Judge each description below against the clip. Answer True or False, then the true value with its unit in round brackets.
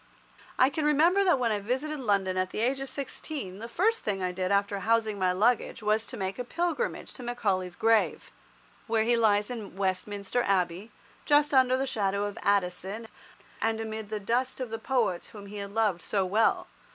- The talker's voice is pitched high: True (220 Hz)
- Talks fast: False (195 wpm)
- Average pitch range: True (4.1 semitones)